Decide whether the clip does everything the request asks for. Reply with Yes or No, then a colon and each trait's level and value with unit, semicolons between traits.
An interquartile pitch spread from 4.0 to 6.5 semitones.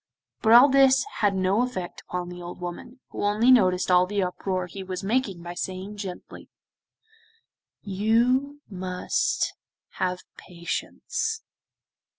Yes: average, 4.7 semitones